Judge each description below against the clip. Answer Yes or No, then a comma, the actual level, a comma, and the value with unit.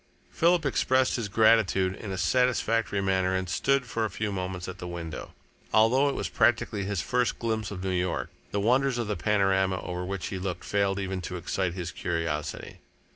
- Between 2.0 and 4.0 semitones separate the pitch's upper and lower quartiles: Yes, average, 3.7 semitones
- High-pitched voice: No, low, 100 Hz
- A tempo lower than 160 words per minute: No, average, 190 wpm